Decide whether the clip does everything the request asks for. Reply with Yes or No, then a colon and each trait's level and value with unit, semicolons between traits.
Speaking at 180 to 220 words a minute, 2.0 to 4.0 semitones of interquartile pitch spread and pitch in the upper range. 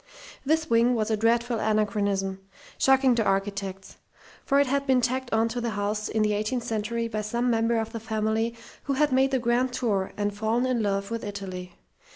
Yes: average, 200 wpm; average, 2.9 semitones; high, 225 Hz